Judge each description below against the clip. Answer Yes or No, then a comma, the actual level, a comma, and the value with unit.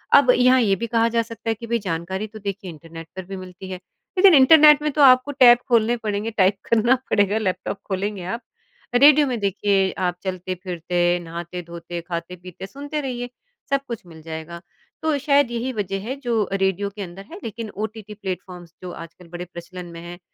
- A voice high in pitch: Yes, high, 200 Hz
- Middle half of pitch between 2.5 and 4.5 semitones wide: No, average, 5.0 semitones